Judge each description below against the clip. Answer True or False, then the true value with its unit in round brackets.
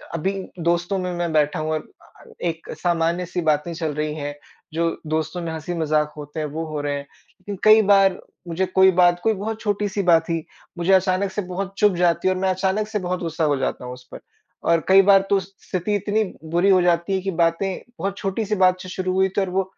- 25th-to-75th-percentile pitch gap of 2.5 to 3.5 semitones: True (3.0 semitones)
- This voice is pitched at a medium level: True (180 Hz)